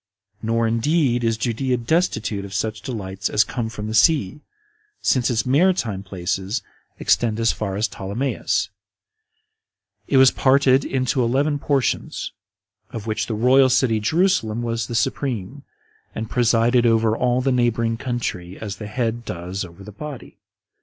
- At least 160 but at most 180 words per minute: No, average, 145 wpm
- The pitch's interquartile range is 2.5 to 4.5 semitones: Yes, average, 3.4 semitones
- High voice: No, low, 115 Hz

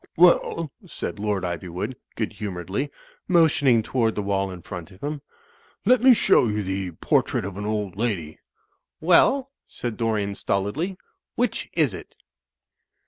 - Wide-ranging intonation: Yes, wide, 7.6 semitones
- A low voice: Yes, low, 105 Hz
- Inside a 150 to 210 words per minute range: Yes, average, 155 wpm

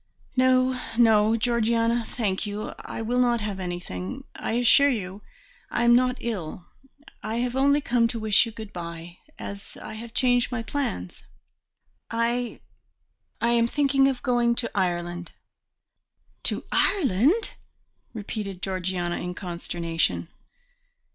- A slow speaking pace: Yes, slow, 130 wpm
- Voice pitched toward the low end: No, high, 230 Hz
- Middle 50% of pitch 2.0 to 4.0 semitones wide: No, average, 4.7 semitones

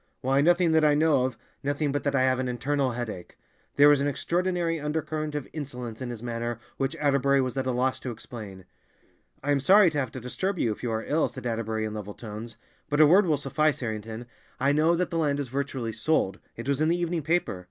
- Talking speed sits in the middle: No, fast, 225 wpm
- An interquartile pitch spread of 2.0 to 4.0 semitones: No, average, 4.4 semitones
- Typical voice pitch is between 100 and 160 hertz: Yes, medium, 140 Hz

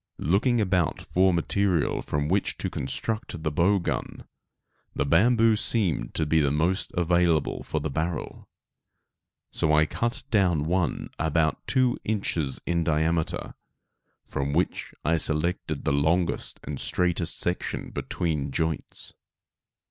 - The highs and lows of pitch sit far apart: No, average, 3.4 semitones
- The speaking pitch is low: Yes, very low, 85 Hz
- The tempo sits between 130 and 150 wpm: Yes, slow, 135 wpm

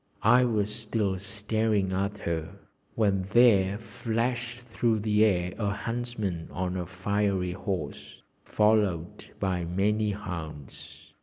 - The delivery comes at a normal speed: No, slow, 120 wpm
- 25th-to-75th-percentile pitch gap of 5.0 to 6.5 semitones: No, average, 3.0 semitones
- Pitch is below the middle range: Yes, low, 100 Hz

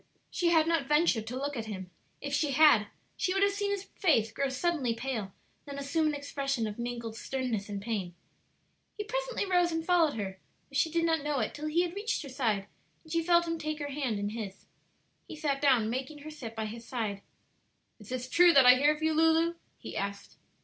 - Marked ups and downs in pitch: Yes, wide, 6.1 semitones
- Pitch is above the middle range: Yes, very high, 280 Hz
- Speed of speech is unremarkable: No, fast, 220 wpm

